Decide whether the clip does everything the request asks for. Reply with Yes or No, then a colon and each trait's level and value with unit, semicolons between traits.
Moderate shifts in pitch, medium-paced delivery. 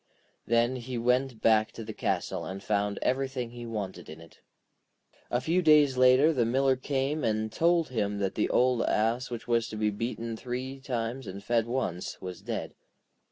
Yes: average, 3.2 semitones; average, 180 wpm